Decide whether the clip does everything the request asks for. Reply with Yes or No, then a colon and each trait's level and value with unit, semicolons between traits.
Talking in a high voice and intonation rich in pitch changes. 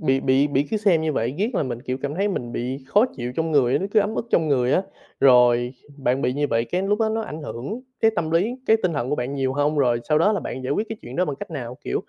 No: medium, 145 Hz; wide, 6.7 semitones